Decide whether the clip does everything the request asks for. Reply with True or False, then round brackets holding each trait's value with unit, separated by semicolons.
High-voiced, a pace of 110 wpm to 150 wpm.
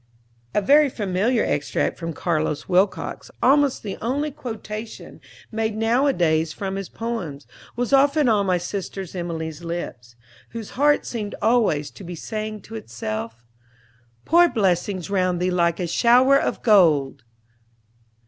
True (200 Hz; 135 wpm)